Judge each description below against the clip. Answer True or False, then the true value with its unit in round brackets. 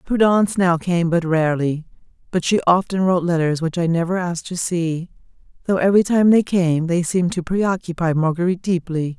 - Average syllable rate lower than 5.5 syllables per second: False (5.6 syllables/s)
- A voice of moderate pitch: True (175 Hz)